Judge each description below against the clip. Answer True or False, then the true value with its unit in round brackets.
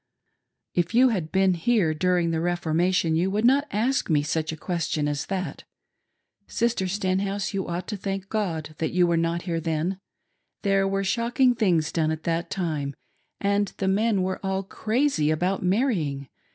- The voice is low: False (185 Hz)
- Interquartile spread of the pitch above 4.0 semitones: False (3.6 semitones)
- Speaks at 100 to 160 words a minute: False (170 wpm)